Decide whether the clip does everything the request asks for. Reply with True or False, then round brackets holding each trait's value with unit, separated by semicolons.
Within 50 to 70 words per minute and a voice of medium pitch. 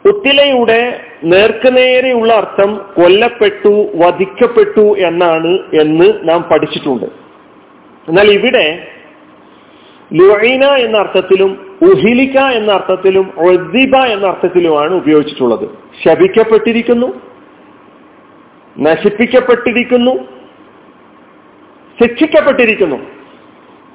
False (60 wpm; 220 Hz)